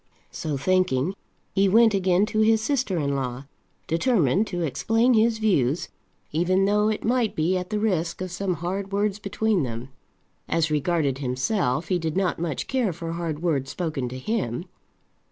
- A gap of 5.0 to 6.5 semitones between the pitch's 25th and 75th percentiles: Yes, wide, 5.5 semitones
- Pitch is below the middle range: No, medium, 180 Hz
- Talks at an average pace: Yes, average, 170 wpm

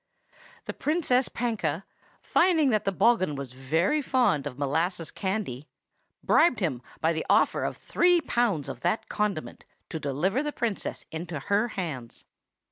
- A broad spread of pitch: Yes, wide, 8.2 semitones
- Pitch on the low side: No, medium, 185 Hz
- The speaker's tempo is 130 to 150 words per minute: Yes, average, 145 wpm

